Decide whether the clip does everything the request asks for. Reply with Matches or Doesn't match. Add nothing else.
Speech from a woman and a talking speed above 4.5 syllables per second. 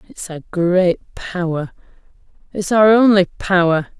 Doesn't match